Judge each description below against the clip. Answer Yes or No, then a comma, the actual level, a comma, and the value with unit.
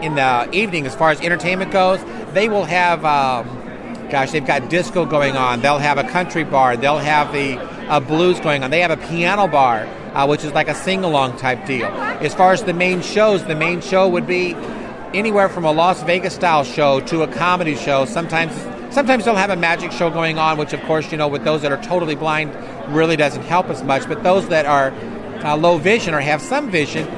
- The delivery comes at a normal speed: No, fast, 215 wpm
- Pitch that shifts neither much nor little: Yes, average, 3.7 semitones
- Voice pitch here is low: No, medium, 160 Hz